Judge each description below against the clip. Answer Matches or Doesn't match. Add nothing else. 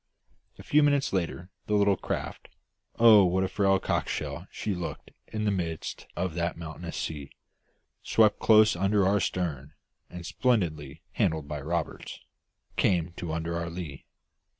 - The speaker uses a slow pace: Doesn't match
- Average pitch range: Matches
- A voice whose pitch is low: Matches